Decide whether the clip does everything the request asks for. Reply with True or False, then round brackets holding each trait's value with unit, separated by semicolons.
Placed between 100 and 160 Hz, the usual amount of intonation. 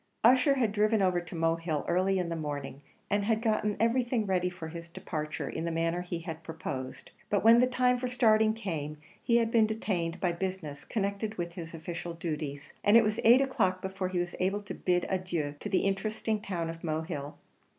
False (185 Hz; 4.6 semitones)